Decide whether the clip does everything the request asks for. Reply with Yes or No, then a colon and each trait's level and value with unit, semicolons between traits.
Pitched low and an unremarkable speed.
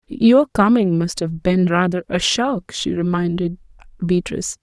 No: high, 190 Hz; average, 145 wpm